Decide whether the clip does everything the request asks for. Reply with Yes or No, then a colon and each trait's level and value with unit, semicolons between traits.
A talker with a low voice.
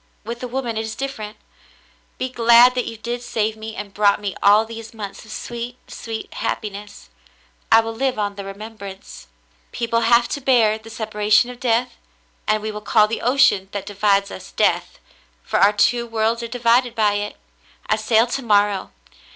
No: high, 220 Hz